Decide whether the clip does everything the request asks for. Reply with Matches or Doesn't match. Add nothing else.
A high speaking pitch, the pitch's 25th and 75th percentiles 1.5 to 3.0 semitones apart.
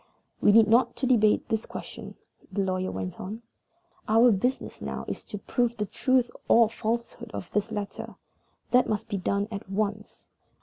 Matches